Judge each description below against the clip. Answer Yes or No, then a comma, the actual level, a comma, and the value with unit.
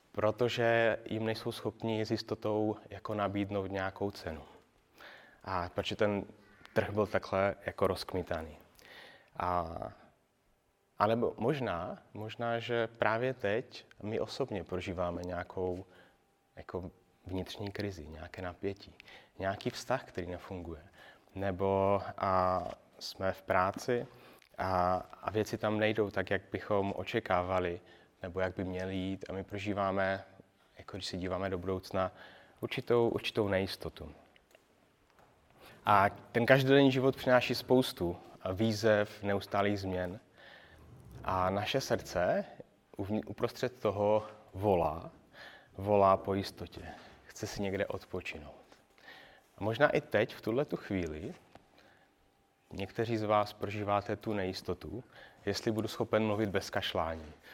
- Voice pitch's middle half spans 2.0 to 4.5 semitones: Yes, narrow, 2.6 semitones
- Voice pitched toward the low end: Yes, low, 100 Hz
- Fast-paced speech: No, slow, 115 wpm